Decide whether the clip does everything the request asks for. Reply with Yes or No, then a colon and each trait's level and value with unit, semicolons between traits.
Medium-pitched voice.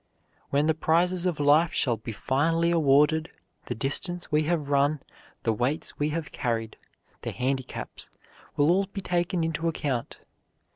Yes: medium, 150 Hz